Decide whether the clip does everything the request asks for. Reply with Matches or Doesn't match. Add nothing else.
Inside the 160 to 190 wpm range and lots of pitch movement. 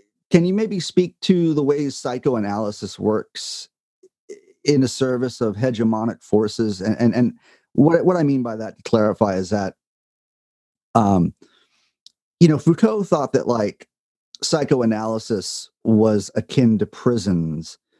Doesn't match